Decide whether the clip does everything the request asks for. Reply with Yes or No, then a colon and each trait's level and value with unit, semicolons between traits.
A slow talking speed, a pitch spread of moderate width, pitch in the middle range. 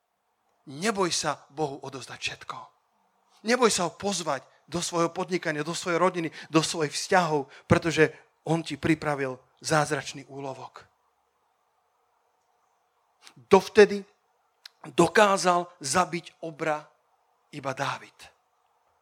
Yes: slow, 95 wpm; average, 3.2 semitones; medium, 165 Hz